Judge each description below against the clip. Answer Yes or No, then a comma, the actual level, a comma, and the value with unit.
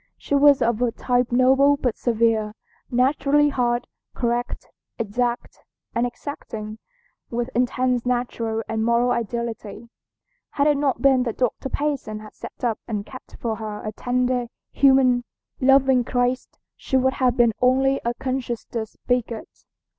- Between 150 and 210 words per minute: No, average, 140 wpm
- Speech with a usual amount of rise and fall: No, narrow, 2.1 semitones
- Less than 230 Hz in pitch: No, high, 245 Hz